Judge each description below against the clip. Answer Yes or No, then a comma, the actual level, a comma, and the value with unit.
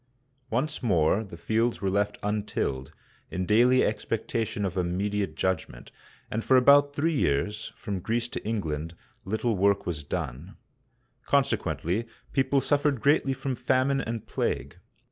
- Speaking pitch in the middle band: No, low, 105 Hz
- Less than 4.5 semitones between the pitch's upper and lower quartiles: No, wide, 5.5 semitones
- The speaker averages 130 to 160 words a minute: Yes, slow, 135 wpm